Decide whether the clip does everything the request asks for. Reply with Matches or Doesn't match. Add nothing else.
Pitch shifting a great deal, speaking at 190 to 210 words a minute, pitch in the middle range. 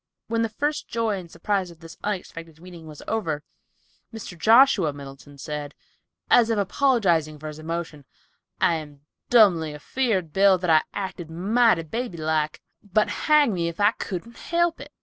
Doesn't match